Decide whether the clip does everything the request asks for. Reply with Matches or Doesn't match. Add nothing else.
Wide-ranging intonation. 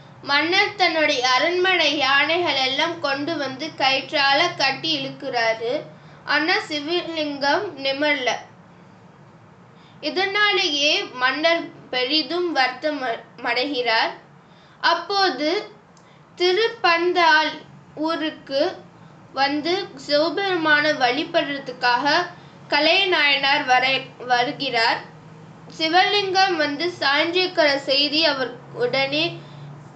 Doesn't match